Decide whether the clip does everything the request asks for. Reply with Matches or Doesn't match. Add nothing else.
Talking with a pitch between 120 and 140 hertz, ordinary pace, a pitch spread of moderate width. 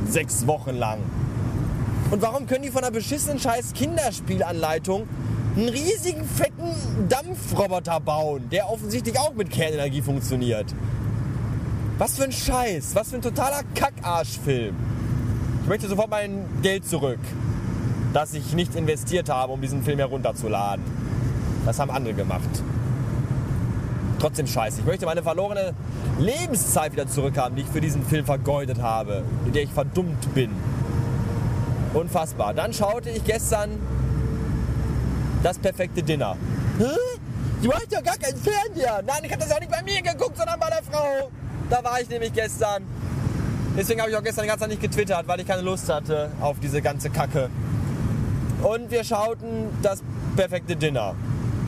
Doesn't match